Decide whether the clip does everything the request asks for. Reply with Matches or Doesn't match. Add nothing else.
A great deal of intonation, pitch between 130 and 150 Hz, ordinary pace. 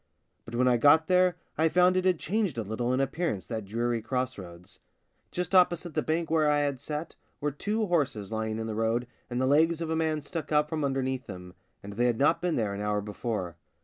Doesn't match